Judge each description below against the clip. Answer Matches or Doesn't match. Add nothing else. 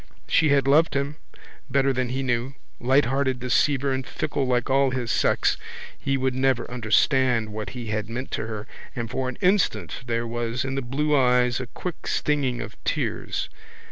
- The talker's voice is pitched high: Doesn't match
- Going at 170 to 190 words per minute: Matches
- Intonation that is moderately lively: Doesn't match